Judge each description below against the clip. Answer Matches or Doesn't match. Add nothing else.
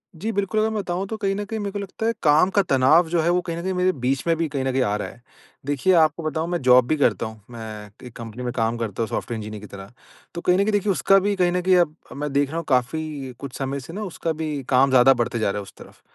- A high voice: Doesn't match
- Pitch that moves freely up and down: Matches